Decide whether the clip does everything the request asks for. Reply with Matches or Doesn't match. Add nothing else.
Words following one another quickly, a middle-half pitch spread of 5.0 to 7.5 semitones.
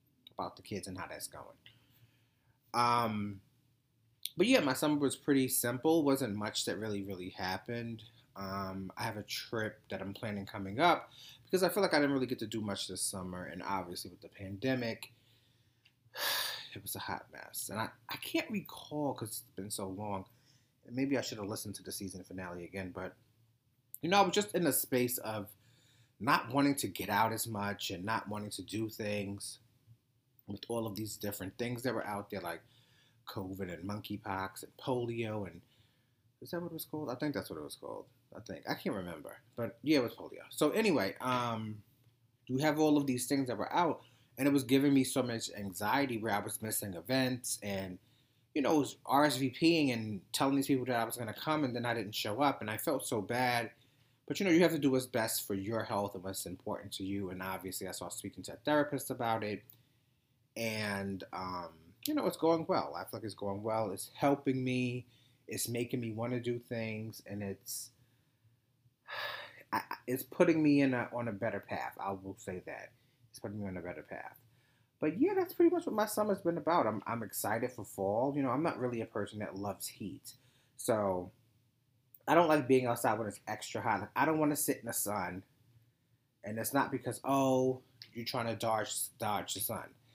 Doesn't match